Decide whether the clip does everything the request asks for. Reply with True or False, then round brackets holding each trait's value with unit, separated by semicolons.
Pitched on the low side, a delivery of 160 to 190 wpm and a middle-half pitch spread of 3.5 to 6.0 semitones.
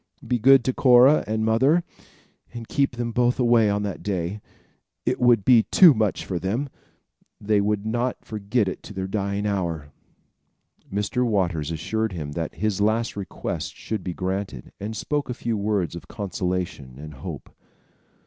True (105 Hz; 165 wpm; 4.1 semitones)